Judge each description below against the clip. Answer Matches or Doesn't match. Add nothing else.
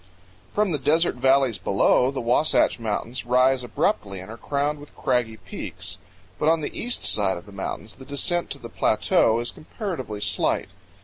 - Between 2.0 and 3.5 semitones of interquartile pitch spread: Doesn't match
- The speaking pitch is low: Matches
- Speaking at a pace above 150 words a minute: Matches